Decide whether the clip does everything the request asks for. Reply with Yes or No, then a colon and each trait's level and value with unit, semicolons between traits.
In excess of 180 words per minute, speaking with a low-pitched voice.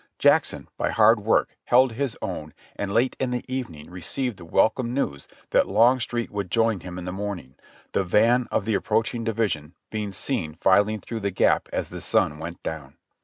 Yes: average, 190 wpm; low, 105 Hz